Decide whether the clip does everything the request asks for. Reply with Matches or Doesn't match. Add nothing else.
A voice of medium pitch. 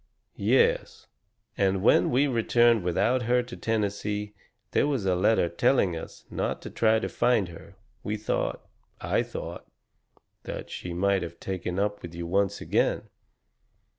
Doesn't match